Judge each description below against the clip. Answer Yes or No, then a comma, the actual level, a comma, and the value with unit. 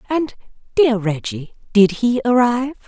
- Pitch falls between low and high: No, high, 230 Hz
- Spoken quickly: No, slow, 105 wpm